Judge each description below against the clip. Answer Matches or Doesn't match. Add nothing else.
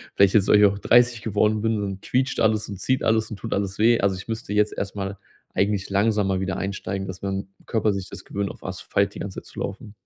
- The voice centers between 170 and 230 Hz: Doesn't match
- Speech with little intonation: Matches